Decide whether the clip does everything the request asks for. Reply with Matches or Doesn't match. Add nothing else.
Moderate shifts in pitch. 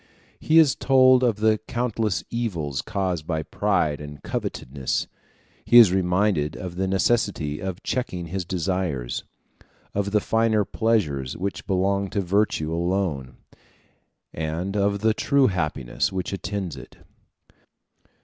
Matches